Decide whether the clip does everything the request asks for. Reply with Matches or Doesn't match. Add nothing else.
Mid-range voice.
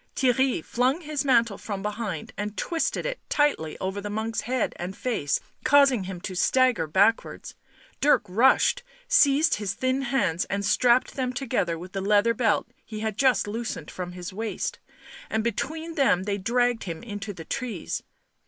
Doesn't match